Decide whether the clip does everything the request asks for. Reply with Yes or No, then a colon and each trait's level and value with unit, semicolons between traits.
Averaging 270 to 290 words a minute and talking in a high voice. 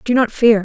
Yes: fast, 280 wpm; high, 230 Hz